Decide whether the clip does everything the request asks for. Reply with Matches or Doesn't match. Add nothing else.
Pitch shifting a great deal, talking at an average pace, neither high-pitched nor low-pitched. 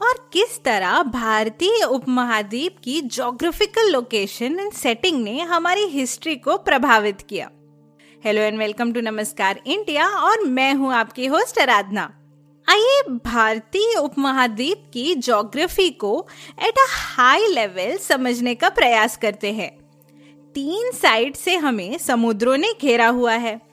Doesn't match